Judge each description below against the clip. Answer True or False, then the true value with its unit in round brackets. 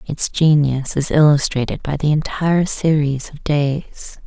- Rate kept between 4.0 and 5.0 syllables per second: True (4.1 syllables/s)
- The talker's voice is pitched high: False (145 Hz)